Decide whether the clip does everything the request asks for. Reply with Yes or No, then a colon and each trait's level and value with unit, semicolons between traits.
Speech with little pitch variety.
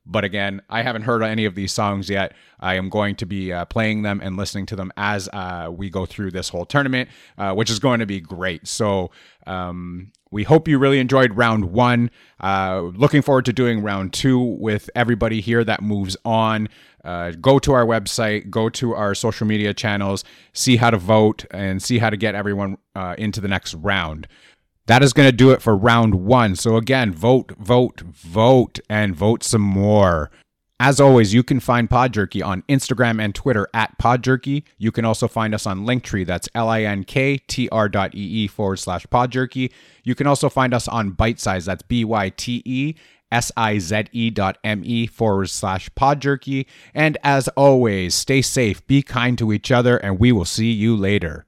No: average, 3.9 semitones